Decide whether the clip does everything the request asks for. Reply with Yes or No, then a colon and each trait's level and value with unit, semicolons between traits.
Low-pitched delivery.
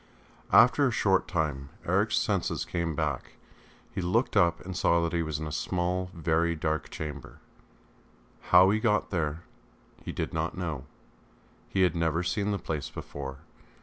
Yes: very low, 85 Hz